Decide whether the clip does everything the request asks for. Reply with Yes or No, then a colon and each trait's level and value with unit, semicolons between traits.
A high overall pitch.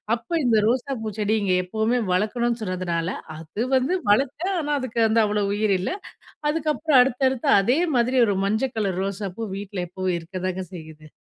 Yes: high, 220 Hz